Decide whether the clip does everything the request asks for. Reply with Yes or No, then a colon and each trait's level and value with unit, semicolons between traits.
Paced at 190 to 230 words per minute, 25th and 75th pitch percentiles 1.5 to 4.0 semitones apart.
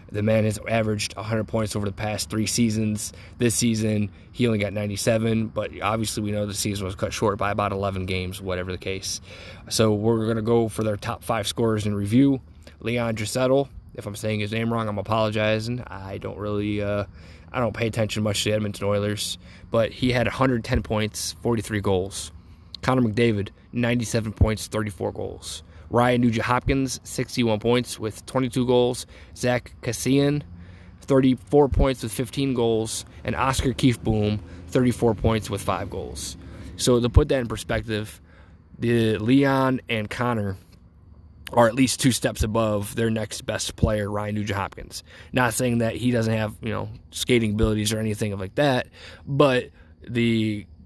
No: average, 170 wpm; average, 3.3 semitones